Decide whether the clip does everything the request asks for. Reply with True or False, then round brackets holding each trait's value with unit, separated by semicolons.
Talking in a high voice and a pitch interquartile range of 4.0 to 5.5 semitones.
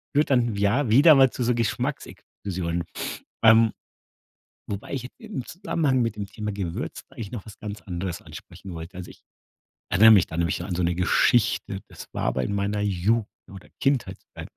False (105 Hz; 4.7 semitones)